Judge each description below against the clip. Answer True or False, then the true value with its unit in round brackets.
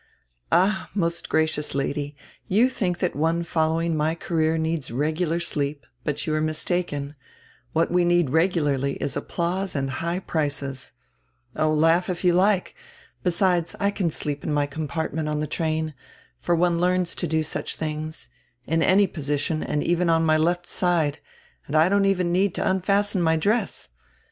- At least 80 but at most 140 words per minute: False (175 wpm)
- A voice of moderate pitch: True (165 Hz)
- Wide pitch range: False (2.7 semitones)